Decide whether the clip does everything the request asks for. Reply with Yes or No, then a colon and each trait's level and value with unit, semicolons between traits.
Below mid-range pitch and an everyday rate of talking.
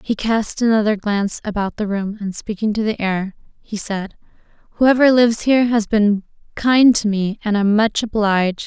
No: high, 215 Hz; average, 180 wpm